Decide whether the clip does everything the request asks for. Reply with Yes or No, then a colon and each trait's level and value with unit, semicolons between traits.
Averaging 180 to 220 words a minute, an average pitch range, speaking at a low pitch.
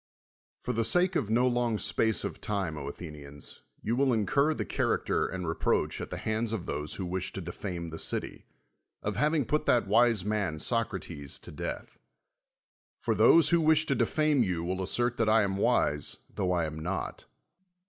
No: average, 185 wpm; wide, 5.8 semitones; low, 105 Hz